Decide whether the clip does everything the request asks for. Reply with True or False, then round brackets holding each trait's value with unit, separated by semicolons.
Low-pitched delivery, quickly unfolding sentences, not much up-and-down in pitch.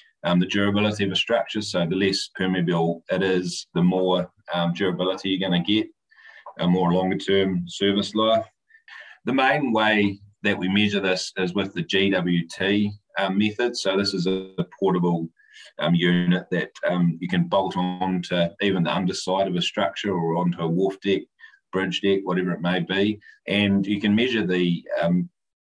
False (95 Hz; 180 wpm; 2.2 semitones)